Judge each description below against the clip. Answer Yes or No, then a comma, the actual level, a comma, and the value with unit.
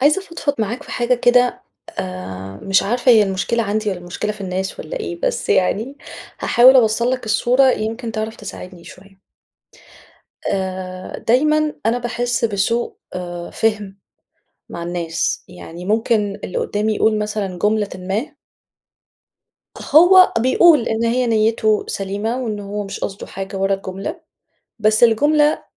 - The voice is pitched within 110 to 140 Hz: No, high, 215 Hz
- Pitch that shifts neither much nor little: Yes, average, 3.9 semitones